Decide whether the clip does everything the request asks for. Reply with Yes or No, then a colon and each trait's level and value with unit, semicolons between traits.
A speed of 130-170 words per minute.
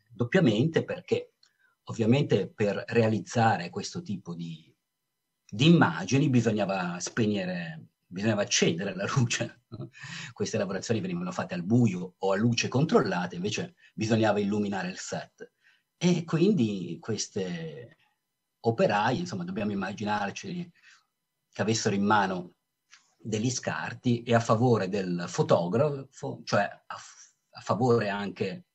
No: slow, 115 wpm